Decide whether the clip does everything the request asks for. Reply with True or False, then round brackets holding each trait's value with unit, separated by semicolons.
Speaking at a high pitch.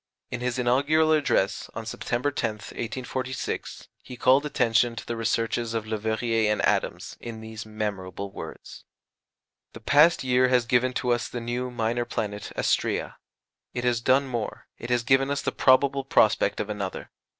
False (120 Hz)